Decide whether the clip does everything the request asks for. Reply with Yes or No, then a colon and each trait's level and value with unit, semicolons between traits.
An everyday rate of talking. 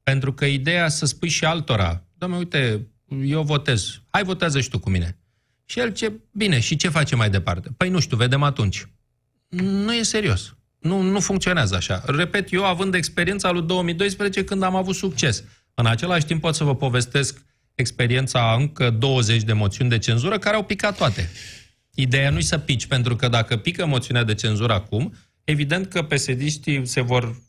No: fast, 185 wpm